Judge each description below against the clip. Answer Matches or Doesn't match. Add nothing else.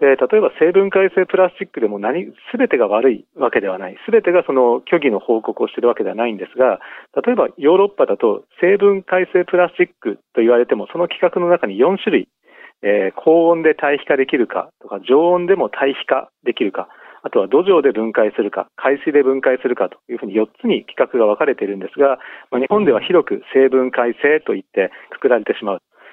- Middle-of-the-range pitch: Matches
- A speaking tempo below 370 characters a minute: Doesn't match